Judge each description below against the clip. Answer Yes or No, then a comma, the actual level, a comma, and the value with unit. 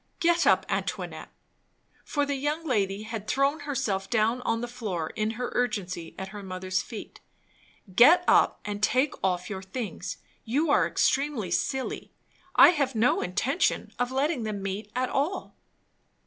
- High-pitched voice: Yes, high, 230 Hz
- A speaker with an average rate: Yes, average, 155 wpm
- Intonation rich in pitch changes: Yes, wide, 5.8 semitones